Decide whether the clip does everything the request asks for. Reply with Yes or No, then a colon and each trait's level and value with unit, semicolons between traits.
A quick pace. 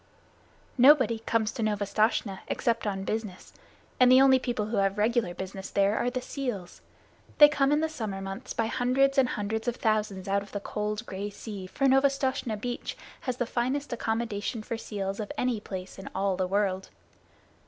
No: average, 180 wpm